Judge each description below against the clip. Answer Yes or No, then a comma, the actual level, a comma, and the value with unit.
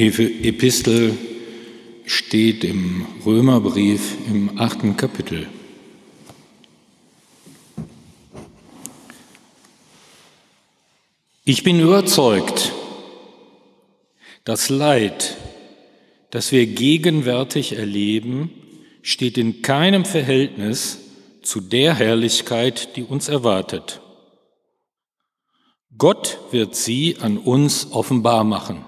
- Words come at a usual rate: No, slow, 70 wpm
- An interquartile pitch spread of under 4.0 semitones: Yes, average, 3.5 semitones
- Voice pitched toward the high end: No, low, 115 Hz